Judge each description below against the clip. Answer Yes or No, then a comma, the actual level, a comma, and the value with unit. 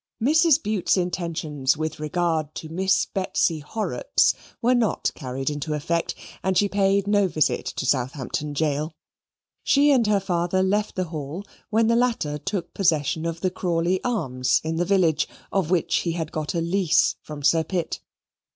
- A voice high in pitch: No, medium, 170 Hz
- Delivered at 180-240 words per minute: No, average, 165 wpm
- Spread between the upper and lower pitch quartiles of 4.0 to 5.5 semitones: Yes, average, 4.3 semitones